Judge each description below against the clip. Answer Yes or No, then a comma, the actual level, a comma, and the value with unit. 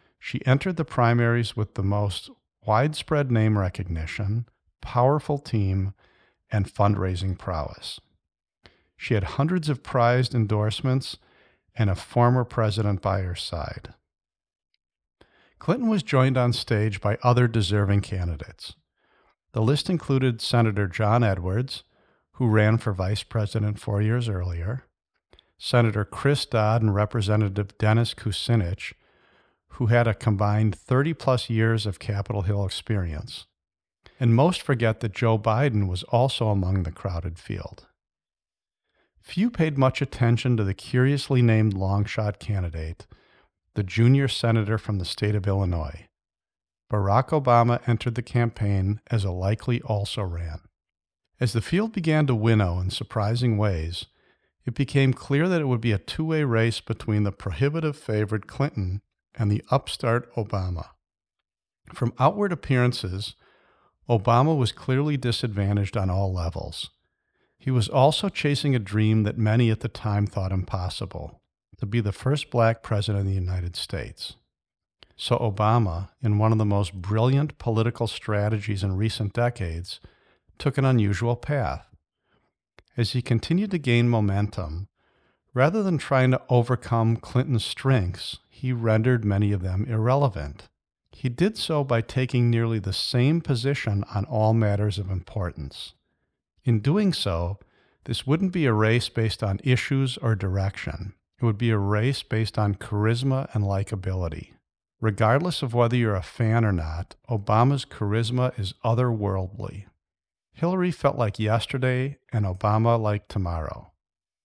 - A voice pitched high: No, low, 110 Hz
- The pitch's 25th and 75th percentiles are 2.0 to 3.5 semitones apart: No, average, 3.9 semitones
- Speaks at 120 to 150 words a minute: Yes, average, 140 wpm